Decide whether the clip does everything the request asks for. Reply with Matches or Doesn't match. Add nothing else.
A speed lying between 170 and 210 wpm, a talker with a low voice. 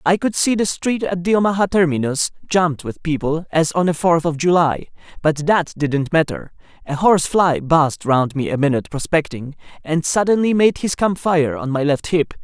Doesn't match